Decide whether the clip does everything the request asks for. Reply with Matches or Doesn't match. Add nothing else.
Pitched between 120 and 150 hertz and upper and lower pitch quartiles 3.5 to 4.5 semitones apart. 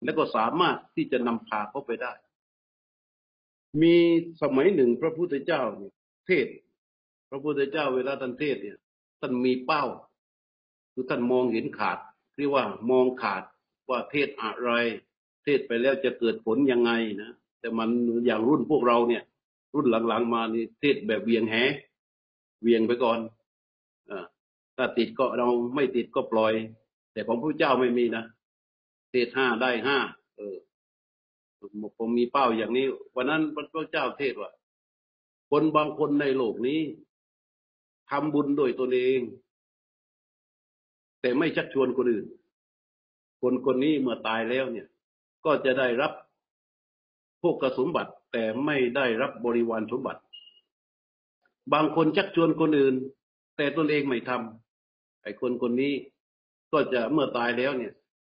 Matches